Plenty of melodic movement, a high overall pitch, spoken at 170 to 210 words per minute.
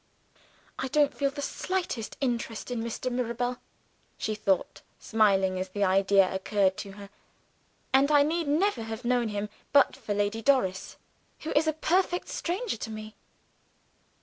No: wide, 5.7 semitones; high, 230 Hz; average, 150 wpm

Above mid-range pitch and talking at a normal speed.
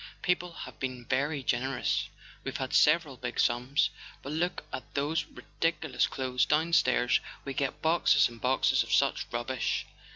No: low, 135 Hz; average, 150 wpm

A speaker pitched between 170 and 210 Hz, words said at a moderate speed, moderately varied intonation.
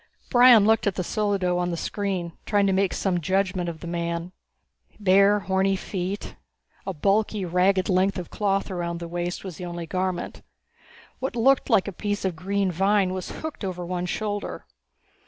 No: high, 190 Hz; average, 175 wpm; narrow, 2.3 semitones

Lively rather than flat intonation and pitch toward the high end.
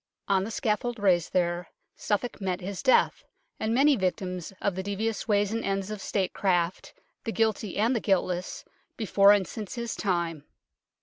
No: average, 3.2 semitones; high, 200 Hz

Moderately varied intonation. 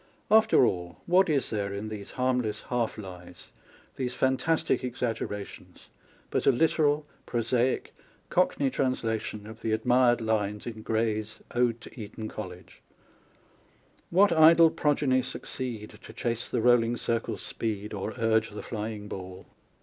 Yes: average, 3.3 semitones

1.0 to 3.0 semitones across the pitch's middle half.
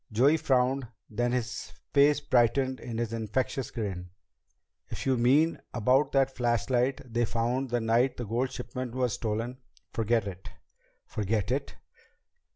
Yes: narrow, 2.5 semitones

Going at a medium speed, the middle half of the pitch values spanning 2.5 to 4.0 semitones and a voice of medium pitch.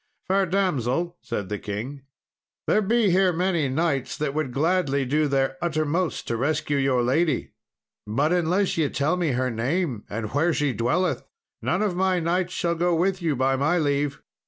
No: average, 175 wpm; average, 4.9 semitones; medium, 155 Hz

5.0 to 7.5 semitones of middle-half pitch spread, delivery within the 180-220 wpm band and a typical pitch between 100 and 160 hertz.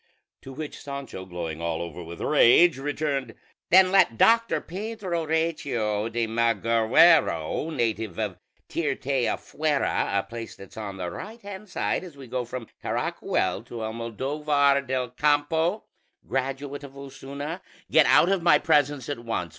No: wide, 5.4 semitones; average, 145 wpm; low, 135 Hz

